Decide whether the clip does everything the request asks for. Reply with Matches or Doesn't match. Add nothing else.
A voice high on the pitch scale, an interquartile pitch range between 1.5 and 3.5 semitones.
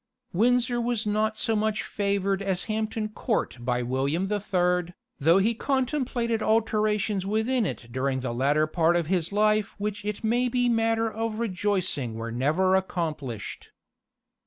Doesn't match